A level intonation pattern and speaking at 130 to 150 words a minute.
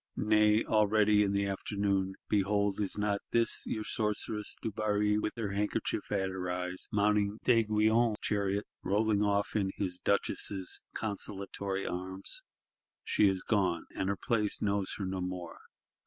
Yes: narrow, 1.7 semitones; average, 140 wpm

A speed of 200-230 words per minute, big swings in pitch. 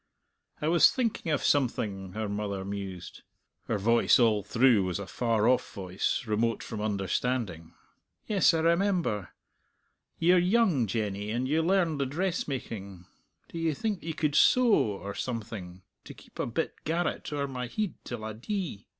No: average, 160 wpm; wide, 8.1 semitones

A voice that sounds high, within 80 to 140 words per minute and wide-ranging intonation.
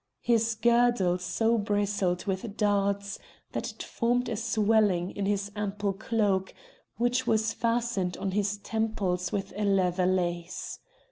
No: high, 205 Hz; slow, 135 wpm; average, 2.9 semitones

